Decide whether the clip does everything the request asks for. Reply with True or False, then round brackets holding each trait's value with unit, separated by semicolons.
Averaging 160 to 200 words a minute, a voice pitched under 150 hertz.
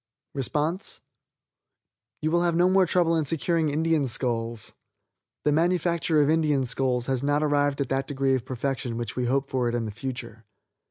True (170 wpm; 140 Hz)